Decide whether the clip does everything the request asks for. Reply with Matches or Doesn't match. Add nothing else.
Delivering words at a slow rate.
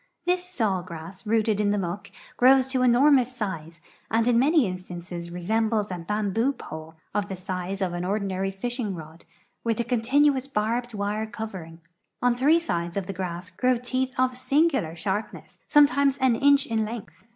Doesn't match